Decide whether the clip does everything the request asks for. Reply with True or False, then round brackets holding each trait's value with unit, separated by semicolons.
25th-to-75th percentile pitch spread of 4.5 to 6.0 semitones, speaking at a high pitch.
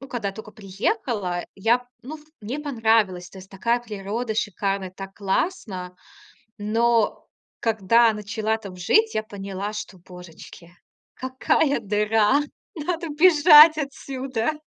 True (4.9 semitones; 220 Hz)